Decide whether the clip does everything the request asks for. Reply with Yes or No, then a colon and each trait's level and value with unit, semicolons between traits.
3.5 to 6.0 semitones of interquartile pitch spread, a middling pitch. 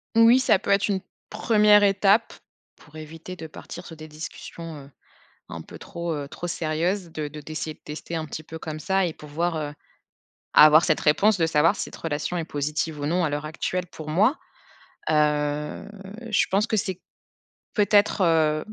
Yes: average, 4.0 semitones; medium, 165 Hz